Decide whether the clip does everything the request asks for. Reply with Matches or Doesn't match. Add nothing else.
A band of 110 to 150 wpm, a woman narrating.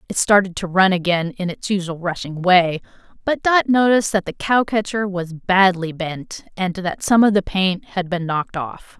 Doesn't match